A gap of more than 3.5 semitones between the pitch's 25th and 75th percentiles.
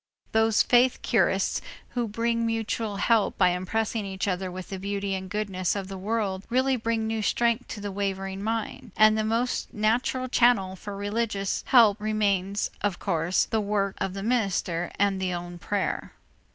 No: average, 2.8 semitones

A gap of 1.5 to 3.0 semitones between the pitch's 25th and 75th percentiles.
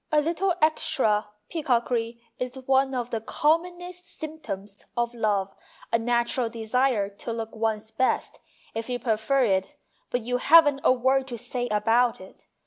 No: average, 3.4 semitones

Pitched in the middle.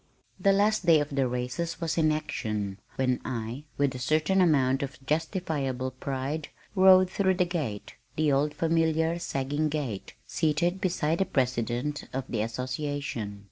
Yes: medium, 145 Hz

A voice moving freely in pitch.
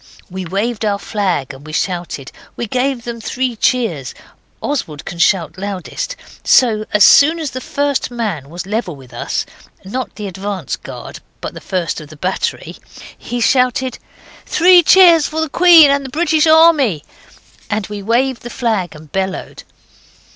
Yes: wide, 6.6 semitones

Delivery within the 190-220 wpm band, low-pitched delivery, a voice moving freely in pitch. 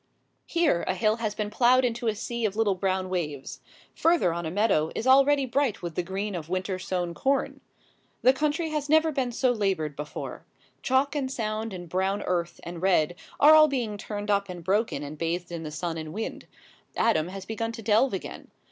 No: average, 200 wpm; high, 205 Hz; wide, 6.1 semitones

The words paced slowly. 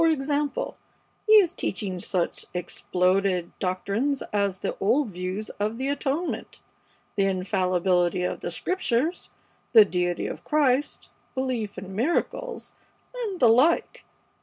Yes: slow, 125 wpm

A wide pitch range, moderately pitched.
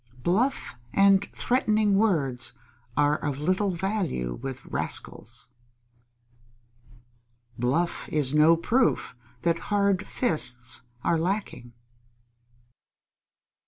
Yes: wide, 7.1 semitones; medium, 165 Hz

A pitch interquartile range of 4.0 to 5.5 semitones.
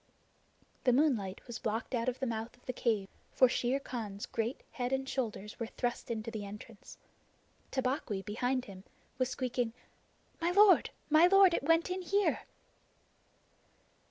No: average, 3.5 semitones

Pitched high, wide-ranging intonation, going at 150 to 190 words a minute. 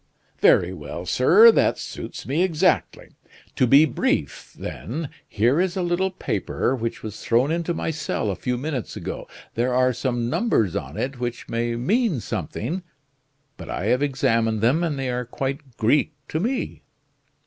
No: low, 135 Hz; wide, 5.8 semitones; average, 165 wpm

